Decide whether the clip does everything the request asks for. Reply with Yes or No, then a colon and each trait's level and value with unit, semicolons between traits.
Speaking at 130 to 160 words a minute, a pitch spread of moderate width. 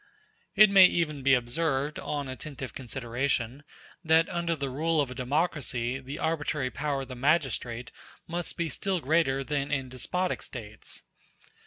Yes: average, 150 wpm; average, 4.0 semitones